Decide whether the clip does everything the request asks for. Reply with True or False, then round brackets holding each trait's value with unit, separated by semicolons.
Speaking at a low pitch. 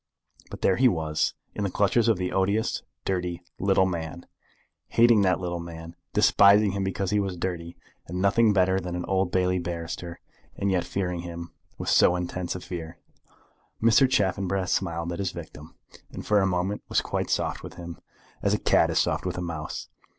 True (90 Hz)